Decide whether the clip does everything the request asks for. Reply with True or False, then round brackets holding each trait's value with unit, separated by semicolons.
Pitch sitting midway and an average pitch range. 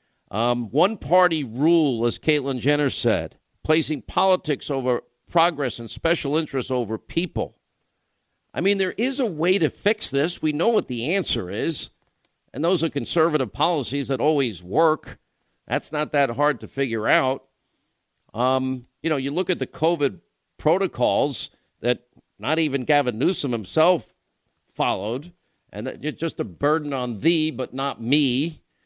True (145 Hz; 4.3 semitones)